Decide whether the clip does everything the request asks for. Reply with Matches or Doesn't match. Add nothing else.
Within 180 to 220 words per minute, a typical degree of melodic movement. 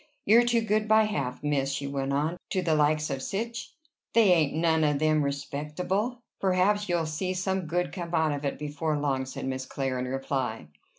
Matches